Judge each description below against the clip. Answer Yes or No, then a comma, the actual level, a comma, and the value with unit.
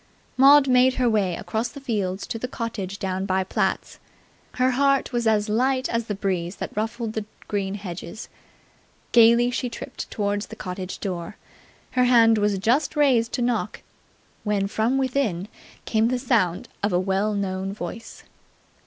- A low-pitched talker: No, high, 220 Hz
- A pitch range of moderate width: Yes, average, 4.0 semitones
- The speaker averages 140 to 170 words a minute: Yes, average, 160 wpm